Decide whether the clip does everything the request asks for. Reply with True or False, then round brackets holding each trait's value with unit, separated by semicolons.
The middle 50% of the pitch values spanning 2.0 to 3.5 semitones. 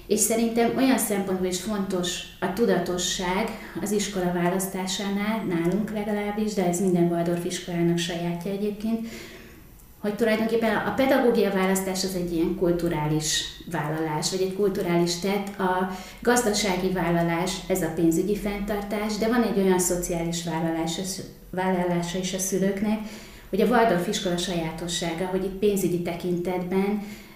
True (2.8 semitones)